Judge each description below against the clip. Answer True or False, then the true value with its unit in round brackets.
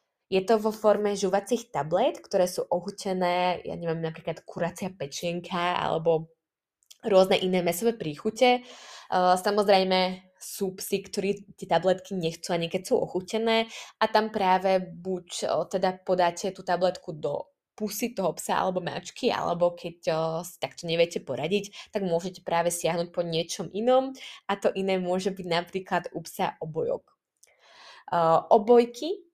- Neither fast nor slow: True (135 wpm)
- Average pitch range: True (3.0 semitones)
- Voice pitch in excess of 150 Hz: True (185 Hz)